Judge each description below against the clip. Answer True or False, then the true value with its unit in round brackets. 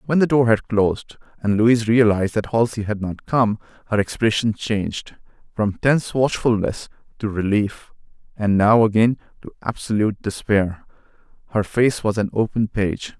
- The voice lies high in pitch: False (110 Hz)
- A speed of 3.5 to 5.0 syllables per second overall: True (4.9 syllables/s)